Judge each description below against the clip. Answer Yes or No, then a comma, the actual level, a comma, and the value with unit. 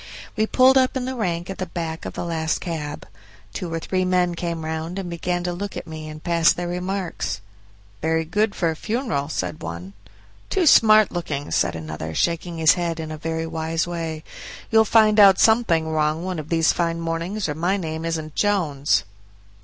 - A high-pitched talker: No, medium, 170 Hz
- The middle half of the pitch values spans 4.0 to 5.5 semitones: No, average, 2.8 semitones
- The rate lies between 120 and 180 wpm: No, average, 195 wpm